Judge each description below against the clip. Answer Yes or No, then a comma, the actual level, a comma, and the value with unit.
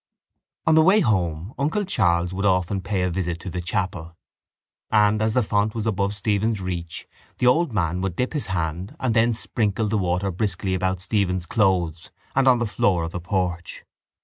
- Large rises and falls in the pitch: No, average, 3.7 semitones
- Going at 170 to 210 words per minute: Yes, average, 190 wpm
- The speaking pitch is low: Yes, very low, 95 Hz